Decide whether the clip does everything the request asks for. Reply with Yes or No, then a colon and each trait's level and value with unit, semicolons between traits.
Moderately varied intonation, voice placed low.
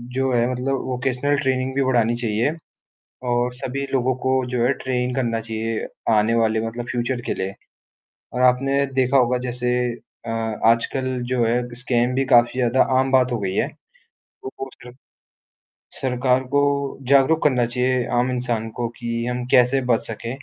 No: narrow, 1.8 semitones; low, 125 Hz